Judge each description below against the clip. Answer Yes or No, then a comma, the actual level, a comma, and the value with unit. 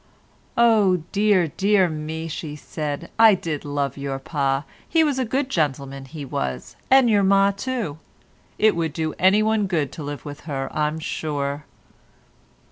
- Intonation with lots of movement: Yes, wide, 6.1 semitones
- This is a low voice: No, medium, 160 Hz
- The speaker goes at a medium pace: Yes, average, 155 wpm